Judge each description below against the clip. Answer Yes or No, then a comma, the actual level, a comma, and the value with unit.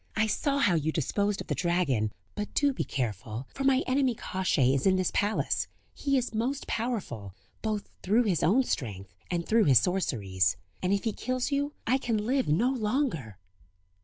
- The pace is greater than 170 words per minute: Yes, average, 185 wpm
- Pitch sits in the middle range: No, high, 205 Hz